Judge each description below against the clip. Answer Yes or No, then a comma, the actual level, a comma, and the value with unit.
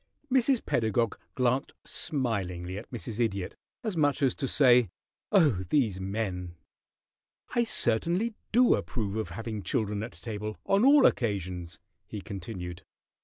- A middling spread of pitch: No, wide, 6.5 semitones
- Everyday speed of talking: No, slow, 130 wpm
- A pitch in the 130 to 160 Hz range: No, low, 115 Hz